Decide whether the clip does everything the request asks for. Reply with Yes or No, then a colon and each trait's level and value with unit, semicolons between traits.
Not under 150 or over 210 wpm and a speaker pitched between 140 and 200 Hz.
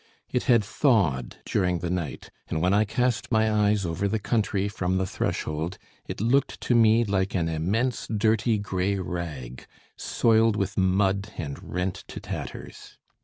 No: average, 160 wpm; low, 100 Hz